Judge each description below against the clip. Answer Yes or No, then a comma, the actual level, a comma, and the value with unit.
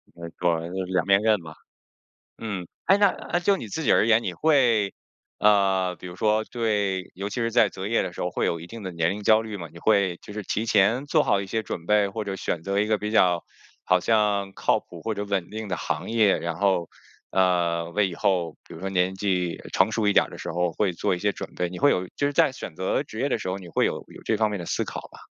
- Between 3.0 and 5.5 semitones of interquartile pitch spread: Yes, average, 3.3 semitones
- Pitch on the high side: No, low, 100 Hz